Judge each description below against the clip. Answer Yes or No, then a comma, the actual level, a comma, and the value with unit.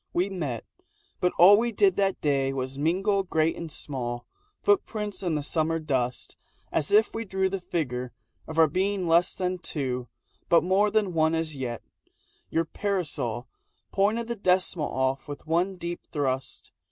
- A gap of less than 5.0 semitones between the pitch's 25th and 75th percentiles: No, wide, 5.5 semitones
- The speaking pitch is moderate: Yes, medium, 165 Hz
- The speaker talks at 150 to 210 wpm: Yes, average, 160 wpm